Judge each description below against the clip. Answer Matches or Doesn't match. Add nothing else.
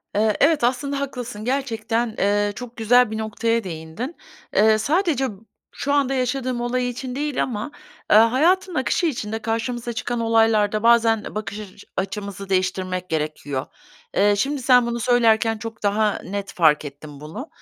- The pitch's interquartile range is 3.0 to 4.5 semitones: Matches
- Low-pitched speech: Doesn't match